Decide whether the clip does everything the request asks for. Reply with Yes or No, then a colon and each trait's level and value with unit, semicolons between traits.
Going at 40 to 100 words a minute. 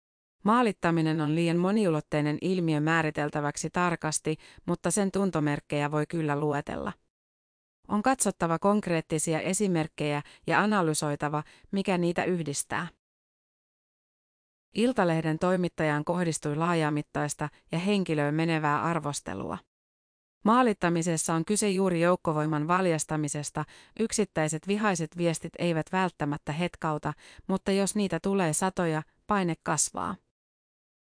Yes: slow, 95 wpm